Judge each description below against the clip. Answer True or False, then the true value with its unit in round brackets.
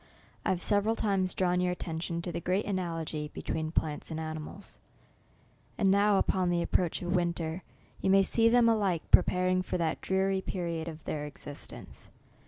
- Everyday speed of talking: True (170 wpm)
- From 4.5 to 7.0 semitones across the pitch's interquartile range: False (2.8 semitones)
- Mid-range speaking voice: True (180 Hz)